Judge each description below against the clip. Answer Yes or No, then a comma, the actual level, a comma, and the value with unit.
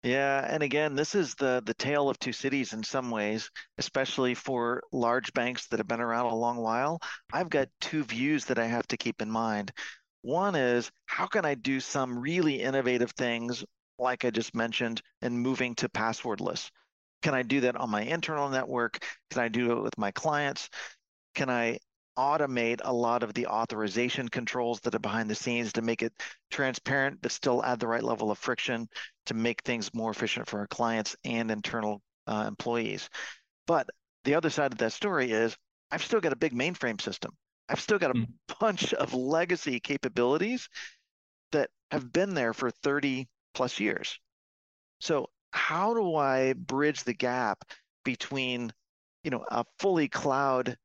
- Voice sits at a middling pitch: No, low, 125 Hz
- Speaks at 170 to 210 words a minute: Yes, average, 180 wpm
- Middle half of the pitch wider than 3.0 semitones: No, narrow, 2.6 semitones